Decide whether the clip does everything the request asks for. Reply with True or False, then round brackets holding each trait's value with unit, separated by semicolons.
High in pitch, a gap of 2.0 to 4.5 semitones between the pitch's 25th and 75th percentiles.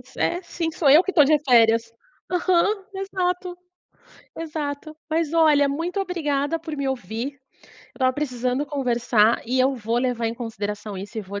False (280 Hz; 5.6 semitones)